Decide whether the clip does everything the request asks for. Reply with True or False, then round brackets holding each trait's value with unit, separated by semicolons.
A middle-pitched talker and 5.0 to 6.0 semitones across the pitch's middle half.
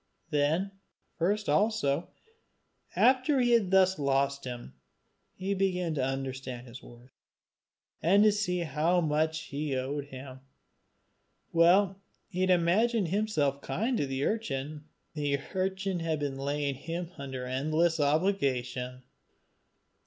True (155 Hz; 5.6 semitones)